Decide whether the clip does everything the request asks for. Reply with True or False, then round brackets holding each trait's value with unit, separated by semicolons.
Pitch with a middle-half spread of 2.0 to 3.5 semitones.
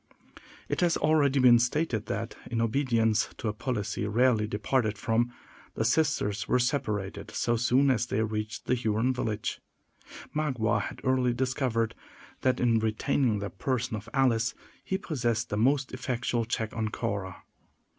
True (3.0 semitones)